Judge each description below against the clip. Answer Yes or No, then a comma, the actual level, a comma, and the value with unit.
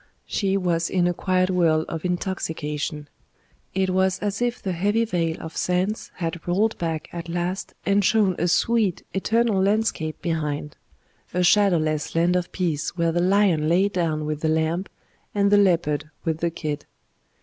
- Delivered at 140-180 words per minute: Yes, average, 165 wpm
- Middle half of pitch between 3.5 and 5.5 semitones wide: No, average, 3.0 semitones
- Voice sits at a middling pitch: Yes, medium, 175 Hz